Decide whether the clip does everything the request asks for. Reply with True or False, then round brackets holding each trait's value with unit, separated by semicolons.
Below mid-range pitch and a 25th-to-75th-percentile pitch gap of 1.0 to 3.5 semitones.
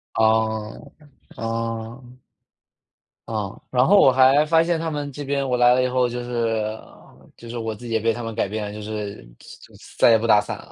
True (115 Hz; 2.8 semitones)